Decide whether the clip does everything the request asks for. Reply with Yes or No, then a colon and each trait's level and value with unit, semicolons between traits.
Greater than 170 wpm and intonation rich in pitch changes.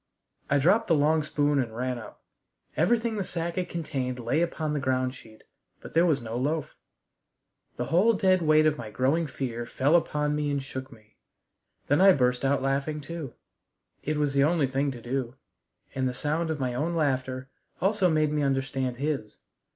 No: average, 190 wpm; average, 3.8 semitones